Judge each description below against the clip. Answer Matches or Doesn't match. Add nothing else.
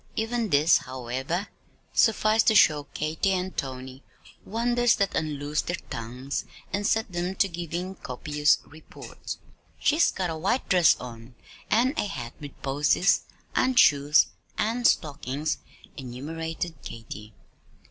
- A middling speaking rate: Doesn't match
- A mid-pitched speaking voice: Matches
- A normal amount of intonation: Doesn't match